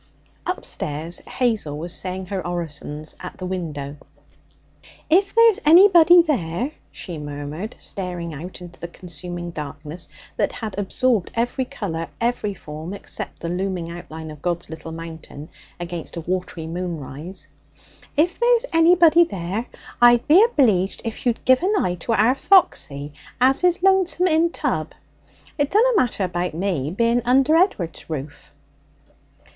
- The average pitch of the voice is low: No, medium, 185 Hz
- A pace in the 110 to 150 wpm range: Yes, average, 140 wpm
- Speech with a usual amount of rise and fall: No, wide, 8.3 semitones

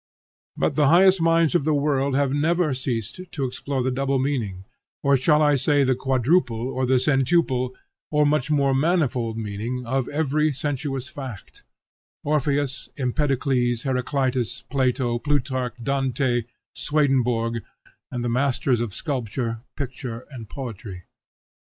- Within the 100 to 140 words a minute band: Yes, slow, 135 wpm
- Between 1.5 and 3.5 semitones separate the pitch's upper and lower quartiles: Yes, average, 2.9 semitones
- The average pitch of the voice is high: No, low, 130 Hz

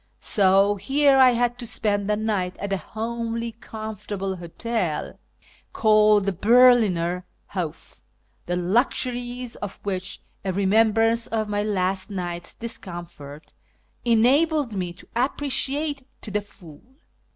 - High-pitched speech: Yes, high, 210 Hz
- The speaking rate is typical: No, slow, 120 wpm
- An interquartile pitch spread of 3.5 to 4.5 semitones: Yes, average, 3.9 semitones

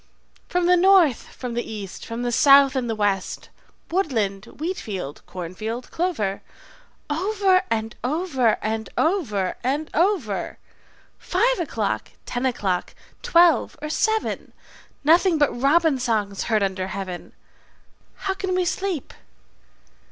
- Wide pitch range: Yes, wide, 8.6 semitones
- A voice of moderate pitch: No, very high, 260 Hz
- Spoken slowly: Yes, slow, 130 wpm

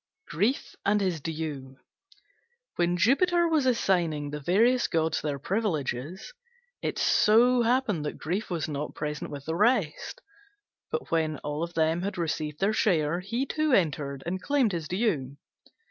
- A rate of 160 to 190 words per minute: No, average, 145 wpm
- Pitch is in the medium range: Yes, medium, 175 Hz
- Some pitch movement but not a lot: No, wide, 6.6 semitones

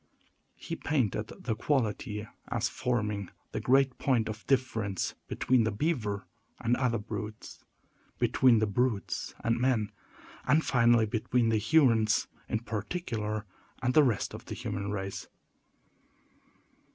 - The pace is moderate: No, slow, 125 wpm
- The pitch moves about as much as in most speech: Yes, average, 3.2 semitones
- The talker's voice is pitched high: No, low, 115 Hz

